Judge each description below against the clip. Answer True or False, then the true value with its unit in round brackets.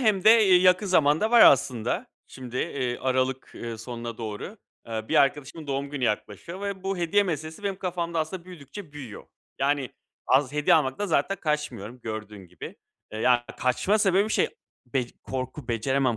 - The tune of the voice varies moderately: False (6.6 semitones)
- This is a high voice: False (140 Hz)